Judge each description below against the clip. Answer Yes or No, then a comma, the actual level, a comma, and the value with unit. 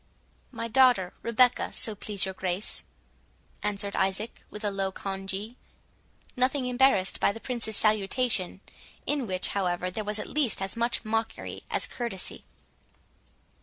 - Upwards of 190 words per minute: No, slow, 135 wpm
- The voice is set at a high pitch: Yes, high, 210 Hz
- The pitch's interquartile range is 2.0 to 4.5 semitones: Yes, average, 3.8 semitones